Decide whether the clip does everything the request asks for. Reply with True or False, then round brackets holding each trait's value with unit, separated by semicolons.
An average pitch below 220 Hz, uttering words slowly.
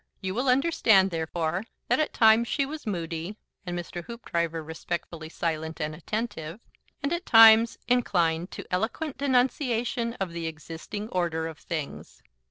False (190 Hz; 145 wpm)